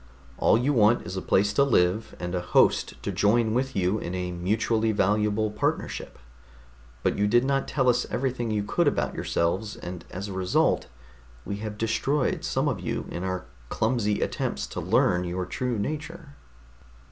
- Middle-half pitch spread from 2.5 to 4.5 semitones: No, average, 4.9 semitones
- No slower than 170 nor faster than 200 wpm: Yes, average, 175 wpm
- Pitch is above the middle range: No, low, 105 Hz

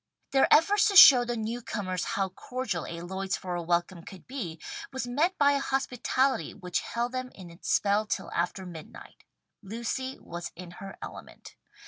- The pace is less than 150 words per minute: No, average, 160 wpm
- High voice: Yes, high, 205 Hz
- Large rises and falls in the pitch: Yes, wide, 6.4 semitones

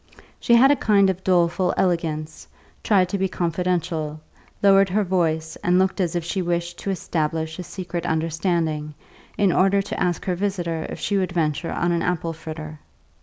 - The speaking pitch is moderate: Yes, medium, 175 Hz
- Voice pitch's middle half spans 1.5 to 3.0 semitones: Yes, average, 2.7 semitones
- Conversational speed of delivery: Yes, average, 175 wpm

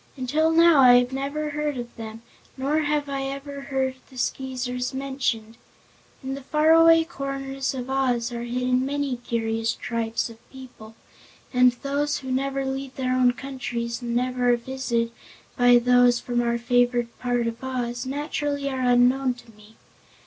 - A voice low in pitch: No, very high, 255 Hz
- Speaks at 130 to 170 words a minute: Yes, average, 160 wpm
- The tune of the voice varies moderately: No, narrow, 2.2 semitones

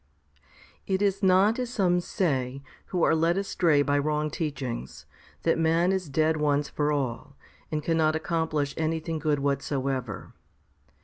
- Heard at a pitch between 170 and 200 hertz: No, medium, 155 Hz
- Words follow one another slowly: No, average, 150 wpm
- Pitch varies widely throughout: No, average, 3.3 semitones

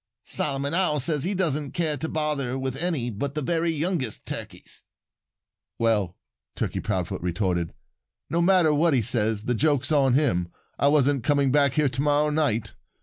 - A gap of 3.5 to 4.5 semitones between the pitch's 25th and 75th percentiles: Yes, average, 4.0 semitones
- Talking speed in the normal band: Yes, average, 165 wpm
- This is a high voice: No, medium, 140 Hz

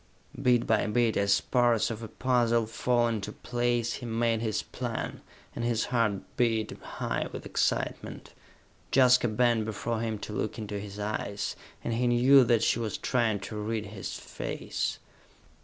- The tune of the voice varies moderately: No, narrow, 2.0 semitones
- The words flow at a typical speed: Yes, average, 160 wpm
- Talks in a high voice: No, low, 115 Hz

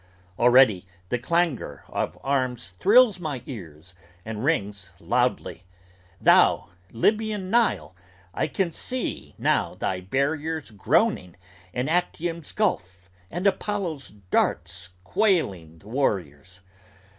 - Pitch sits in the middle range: No, low, 130 Hz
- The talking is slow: Yes, slow, 105 wpm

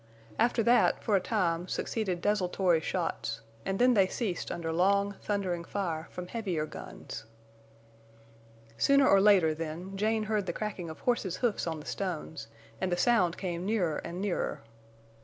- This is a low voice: No, medium, 185 Hz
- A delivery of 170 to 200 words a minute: No, average, 160 wpm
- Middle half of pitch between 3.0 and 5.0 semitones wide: Yes, average, 3.7 semitones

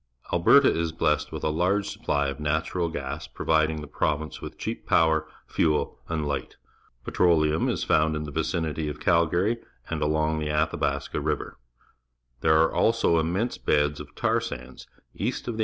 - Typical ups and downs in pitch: No, narrow, 1.8 semitones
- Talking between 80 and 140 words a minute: No, average, 175 wpm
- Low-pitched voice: Yes, very low, 80 Hz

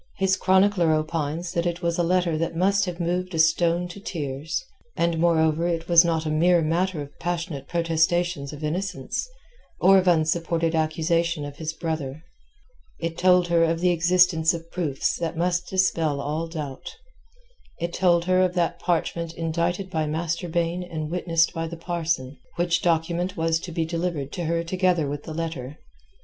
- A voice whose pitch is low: No, medium, 170 Hz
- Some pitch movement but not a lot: No, narrow, 1.7 semitones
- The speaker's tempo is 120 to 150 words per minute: No, average, 175 wpm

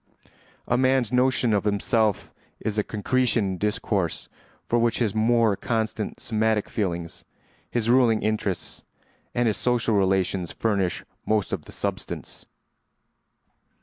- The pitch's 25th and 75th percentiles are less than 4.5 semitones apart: Yes, average, 2.9 semitones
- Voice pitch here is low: Yes, low, 110 Hz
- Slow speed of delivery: Yes, slow, 125 wpm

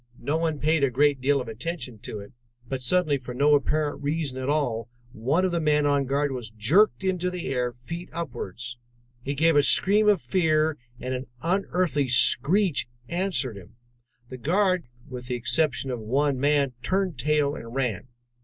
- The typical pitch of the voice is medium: Yes, medium, 145 Hz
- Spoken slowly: No, average, 180 wpm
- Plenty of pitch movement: No, average, 4.6 semitones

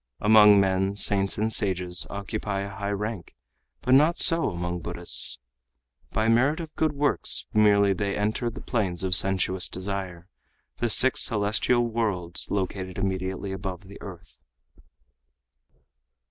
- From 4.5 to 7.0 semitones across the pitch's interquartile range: No, average, 2.7 semitones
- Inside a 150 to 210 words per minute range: No, slow, 135 wpm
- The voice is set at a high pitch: No, low, 100 Hz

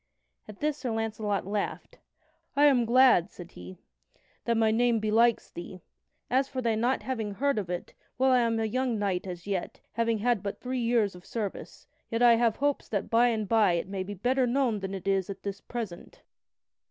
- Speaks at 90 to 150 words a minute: No, average, 200 wpm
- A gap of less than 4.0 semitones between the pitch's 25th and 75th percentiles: Yes, average, 3.6 semitones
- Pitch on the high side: Yes, high, 225 Hz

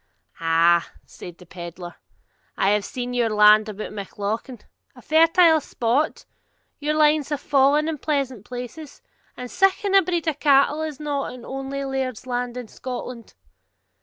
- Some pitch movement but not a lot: No, wide, 5.8 semitones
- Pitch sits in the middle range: No, very high, 260 Hz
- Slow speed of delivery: No, average, 150 wpm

